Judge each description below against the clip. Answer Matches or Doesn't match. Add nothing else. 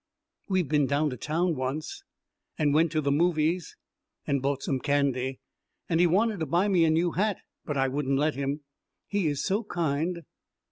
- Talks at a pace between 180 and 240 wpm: Matches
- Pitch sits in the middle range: Matches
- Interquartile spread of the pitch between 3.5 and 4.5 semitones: Matches